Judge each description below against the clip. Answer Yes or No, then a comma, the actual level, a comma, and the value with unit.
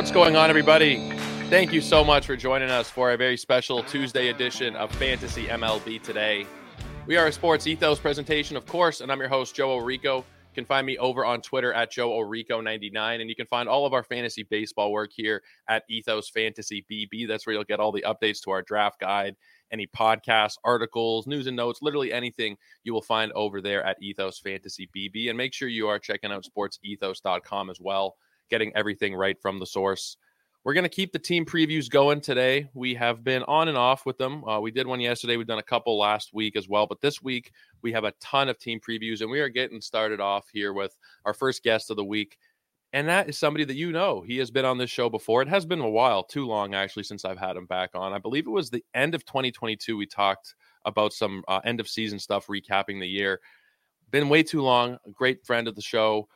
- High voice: No, low, 115 Hz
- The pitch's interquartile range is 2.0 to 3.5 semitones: No, average, 4.0 semitones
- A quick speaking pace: Yes, fast, 230 wpm